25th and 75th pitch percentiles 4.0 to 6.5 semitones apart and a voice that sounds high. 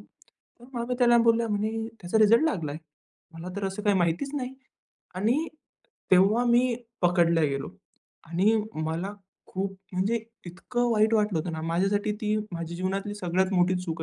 Yes: average, 4.4 semitones; high, 195 Hz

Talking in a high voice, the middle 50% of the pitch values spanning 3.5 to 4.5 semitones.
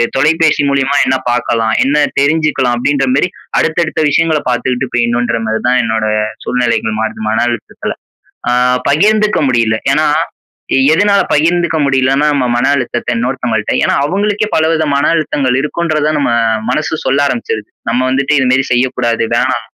No: low, 135 Hz; average, 4.2 semitones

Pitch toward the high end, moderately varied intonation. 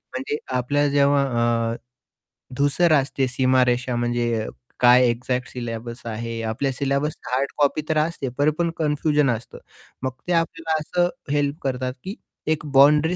No: low, 135 Hz; average, 3.2 semitones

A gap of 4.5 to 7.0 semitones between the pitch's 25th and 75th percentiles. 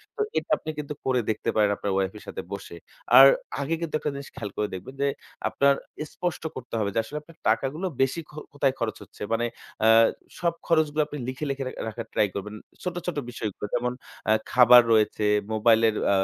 Yes: average, 5.3 semitones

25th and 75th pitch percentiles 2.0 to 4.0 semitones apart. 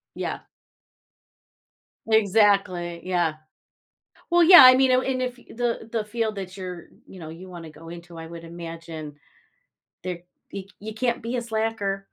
No: average, 5.2 semitones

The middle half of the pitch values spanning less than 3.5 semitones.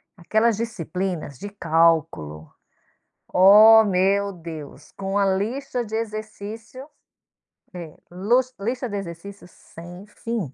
No: average, 4.5 semitones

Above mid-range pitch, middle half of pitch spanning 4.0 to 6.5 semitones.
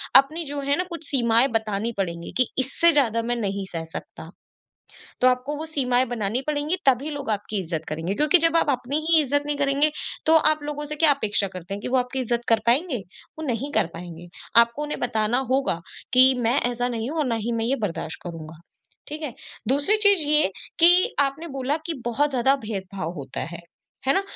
Yes: very high, 255 Hz; average, 5.3 semitones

